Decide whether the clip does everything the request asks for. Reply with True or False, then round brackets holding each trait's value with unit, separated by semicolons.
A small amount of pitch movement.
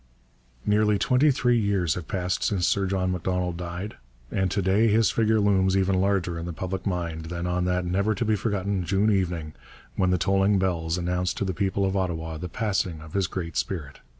True (2.3 semitones)